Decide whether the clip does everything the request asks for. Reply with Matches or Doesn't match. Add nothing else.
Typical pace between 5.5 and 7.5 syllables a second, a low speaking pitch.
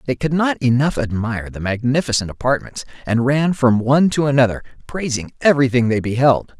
Matches